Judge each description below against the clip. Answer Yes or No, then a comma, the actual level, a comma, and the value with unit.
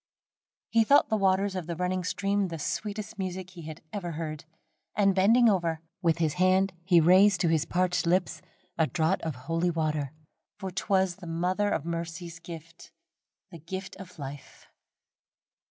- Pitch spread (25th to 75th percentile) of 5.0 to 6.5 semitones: No, narrow, 2.6 semitones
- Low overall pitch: No, medium, 180 Hz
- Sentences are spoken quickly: No, average, 165 wpm